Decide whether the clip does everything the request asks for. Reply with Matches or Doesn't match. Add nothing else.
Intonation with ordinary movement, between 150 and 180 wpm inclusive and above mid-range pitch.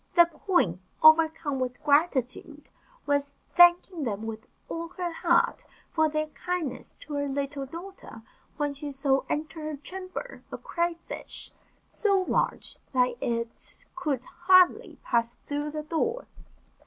Doesn't match